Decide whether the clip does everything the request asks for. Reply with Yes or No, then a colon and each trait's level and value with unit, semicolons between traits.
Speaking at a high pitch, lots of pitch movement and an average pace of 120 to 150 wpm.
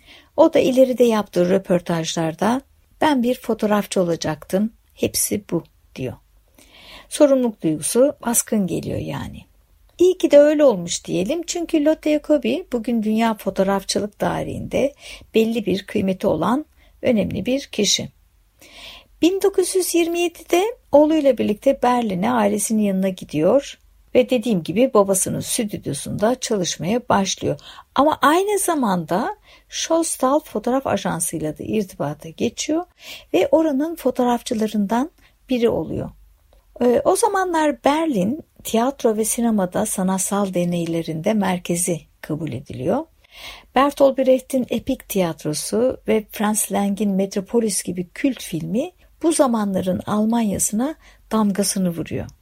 No: high, 230 Hz; wide, 6.3 semitones; average, 105 wpm